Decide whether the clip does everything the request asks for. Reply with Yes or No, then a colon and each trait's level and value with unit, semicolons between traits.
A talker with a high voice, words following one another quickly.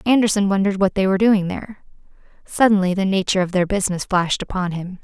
No: high, 195 Hz; average, 190 wpm